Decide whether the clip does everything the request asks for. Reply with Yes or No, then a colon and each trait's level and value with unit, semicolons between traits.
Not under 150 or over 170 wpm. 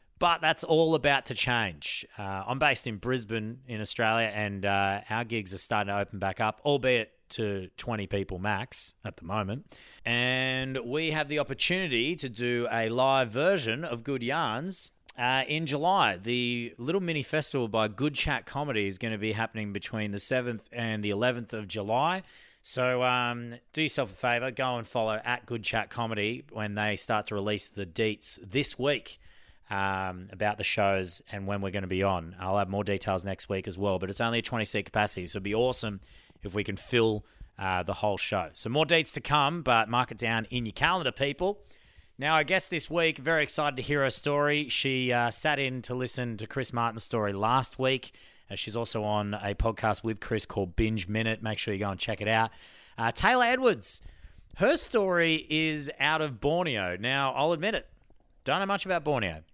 No: average, 200 wpm